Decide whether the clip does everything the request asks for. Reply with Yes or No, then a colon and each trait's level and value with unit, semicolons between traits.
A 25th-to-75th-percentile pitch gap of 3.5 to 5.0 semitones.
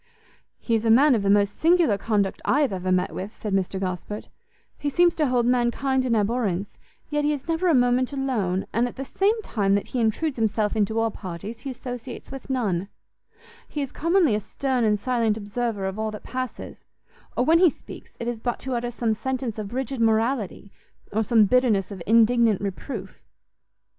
Yes: average, 4.1 semitones